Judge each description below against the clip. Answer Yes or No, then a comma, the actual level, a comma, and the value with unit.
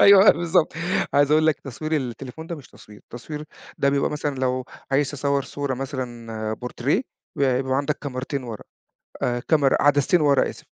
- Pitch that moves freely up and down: No, average, 2.7 semitones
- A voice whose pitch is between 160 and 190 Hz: No, medium, 140 Hz